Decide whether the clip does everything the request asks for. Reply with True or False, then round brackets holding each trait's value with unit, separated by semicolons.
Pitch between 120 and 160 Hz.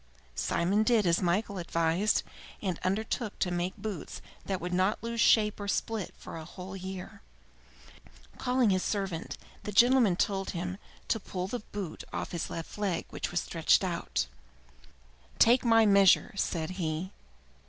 False (195 Hz)